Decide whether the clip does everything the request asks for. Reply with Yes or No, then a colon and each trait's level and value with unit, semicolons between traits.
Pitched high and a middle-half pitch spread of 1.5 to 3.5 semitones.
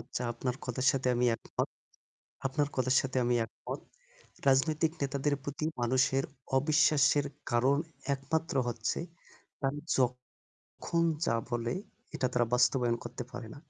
No: low, 130 Hz; narrow, 2.6 semitones